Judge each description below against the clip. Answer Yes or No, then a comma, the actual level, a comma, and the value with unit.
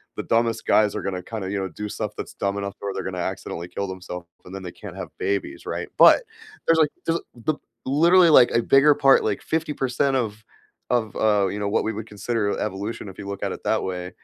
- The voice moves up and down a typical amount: Yes, average, 4.2 semitones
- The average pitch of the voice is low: Yes, low, 105 Hz